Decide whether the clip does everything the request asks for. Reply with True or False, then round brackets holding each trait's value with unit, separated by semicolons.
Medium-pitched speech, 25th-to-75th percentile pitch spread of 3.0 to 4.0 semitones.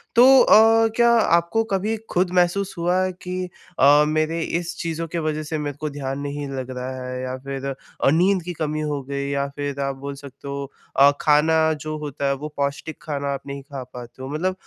True (150 Hz; 3.7 semitones)